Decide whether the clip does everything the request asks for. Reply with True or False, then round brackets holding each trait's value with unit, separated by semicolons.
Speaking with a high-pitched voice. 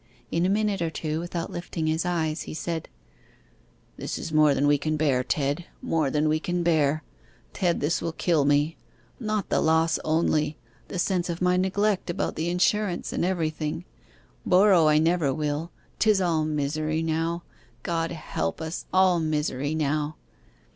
False (160 Hz)